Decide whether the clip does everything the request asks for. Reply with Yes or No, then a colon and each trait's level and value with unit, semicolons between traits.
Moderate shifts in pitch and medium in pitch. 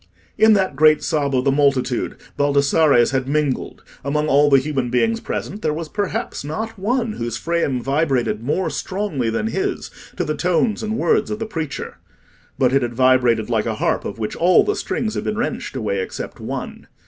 No: wide, 7.4 semitones; medium, 150 Hz